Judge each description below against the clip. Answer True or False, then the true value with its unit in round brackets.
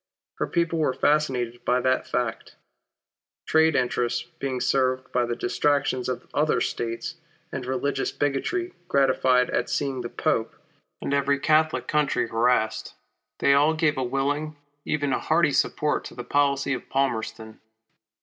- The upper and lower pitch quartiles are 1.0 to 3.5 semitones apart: True (3.0 semitones)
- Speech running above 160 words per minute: False (145 wpm)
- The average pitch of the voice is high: False (135 Hz)